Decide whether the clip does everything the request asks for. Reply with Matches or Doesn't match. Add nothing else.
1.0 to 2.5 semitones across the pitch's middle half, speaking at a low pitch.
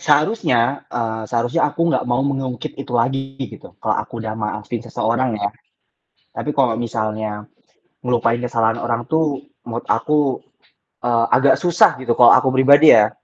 Doesn't match